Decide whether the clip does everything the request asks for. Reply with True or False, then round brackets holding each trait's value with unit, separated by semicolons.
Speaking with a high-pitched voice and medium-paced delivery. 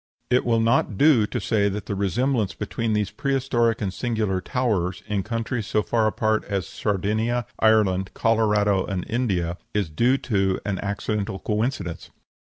False (105 Hz; 155 wpm)